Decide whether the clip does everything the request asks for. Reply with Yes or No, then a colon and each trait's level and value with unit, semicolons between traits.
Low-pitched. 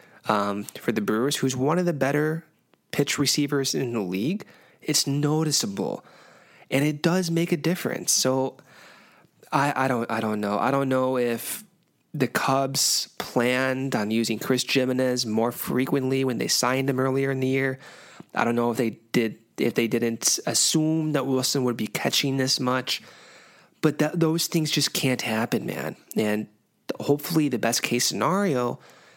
Yes: low, 130 Hz